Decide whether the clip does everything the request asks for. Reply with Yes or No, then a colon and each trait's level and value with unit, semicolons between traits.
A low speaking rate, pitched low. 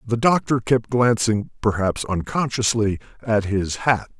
Yes: slow, 130 wpm; low, 110 Hz